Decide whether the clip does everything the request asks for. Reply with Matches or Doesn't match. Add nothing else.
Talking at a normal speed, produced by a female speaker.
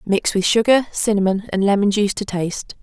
Matches